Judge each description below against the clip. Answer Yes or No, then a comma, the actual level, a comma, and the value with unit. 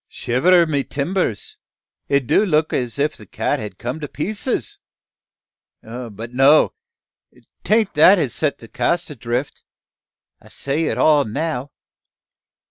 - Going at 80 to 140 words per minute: Yes, slow, 135 wpm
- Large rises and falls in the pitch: No, average, 4.5 semitones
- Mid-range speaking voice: Yes, medium, 145 Hz